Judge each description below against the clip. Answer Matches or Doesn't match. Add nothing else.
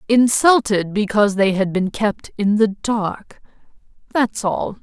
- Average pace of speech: Doesn't match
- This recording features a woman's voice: Matches